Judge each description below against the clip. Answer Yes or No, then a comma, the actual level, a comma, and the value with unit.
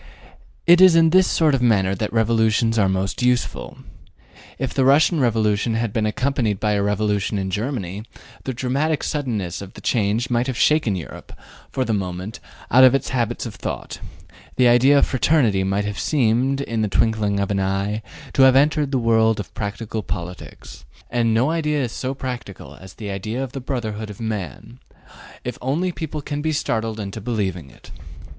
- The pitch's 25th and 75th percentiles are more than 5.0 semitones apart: No, average, 4.4 semitones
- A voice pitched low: Yes, low, 115 Hz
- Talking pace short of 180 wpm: No, average, 185 wpm